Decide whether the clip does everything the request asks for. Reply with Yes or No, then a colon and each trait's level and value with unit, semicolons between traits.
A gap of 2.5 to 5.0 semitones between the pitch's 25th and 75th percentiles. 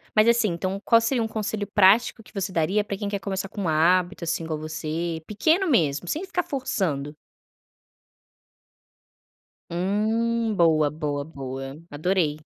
No: wide, 5.5 semitones